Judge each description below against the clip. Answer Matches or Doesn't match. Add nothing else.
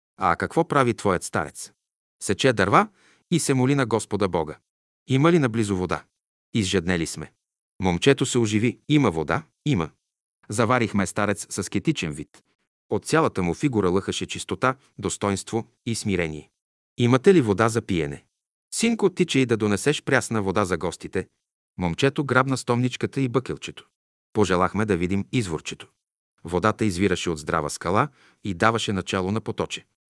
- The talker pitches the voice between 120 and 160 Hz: Doesn't match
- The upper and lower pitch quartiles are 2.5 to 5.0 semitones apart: Doesn't match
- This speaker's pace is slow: Doesn't match